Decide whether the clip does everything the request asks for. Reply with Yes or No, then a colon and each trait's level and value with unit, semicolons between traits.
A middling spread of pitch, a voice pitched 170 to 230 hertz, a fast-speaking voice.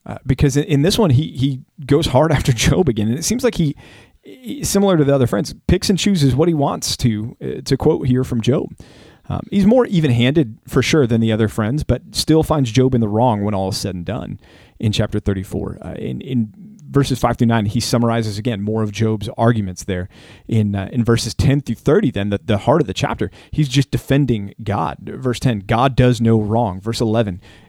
No: average, 4.6 semitones; low, 120 Hz; fast, 225 wpm